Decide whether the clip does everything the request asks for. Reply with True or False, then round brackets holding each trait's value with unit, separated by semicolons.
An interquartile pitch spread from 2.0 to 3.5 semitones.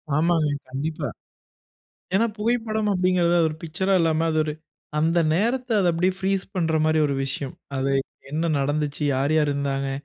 False (4.1 semitones)